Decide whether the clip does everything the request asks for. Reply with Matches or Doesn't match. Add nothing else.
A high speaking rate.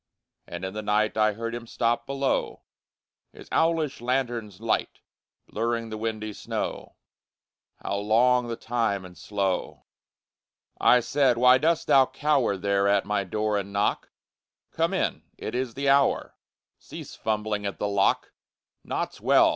Doesn't match